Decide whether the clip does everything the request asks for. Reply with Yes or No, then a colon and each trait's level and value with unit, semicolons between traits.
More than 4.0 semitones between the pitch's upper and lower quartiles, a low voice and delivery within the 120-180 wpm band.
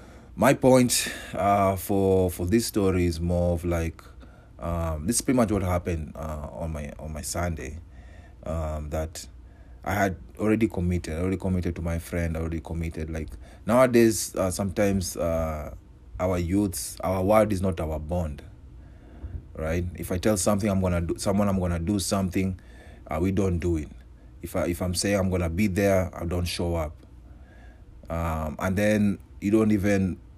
No: average, 3.3 semitones; very low, 90 Hz; average, 170 wpm